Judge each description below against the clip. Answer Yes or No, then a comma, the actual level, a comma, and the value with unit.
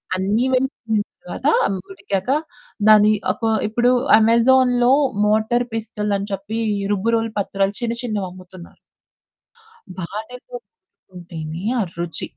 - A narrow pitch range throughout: No, average, 3.7 semitones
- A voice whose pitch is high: Yes, high, 215 Hz